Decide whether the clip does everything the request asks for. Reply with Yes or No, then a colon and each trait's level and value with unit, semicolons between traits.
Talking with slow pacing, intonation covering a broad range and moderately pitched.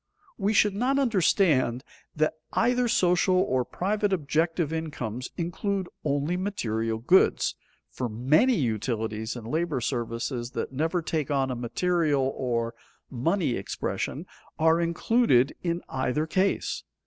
Yes: slow, 125 wpm; wide, 6.7 semitones; medium, 155 Hz